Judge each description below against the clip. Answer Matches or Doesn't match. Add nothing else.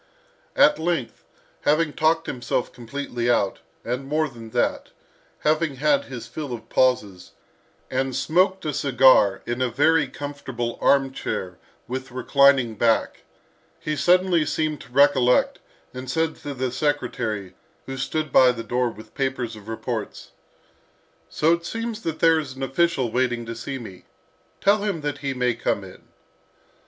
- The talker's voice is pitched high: Doesn't match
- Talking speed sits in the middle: Matches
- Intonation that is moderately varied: Matches